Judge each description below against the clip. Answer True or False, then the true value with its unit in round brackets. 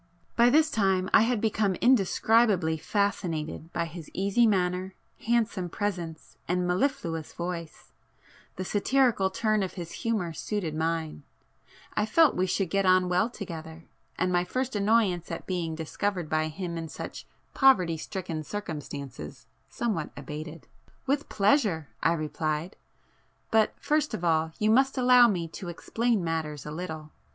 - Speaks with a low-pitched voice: False (180 Hz)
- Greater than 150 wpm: False (135 wpm)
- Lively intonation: False (4.9 semitones)